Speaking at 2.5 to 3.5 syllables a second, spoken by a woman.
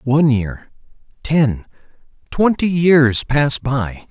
No: 3.1 syllables/s; male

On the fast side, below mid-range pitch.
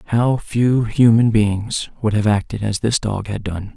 No: average, 190 wpm; low, 110 Hz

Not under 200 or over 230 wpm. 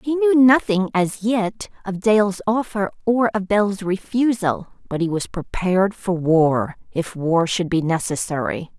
No: average, 155 wpm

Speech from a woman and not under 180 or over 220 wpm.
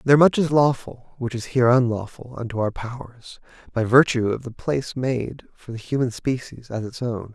No: male; average, 195 wpm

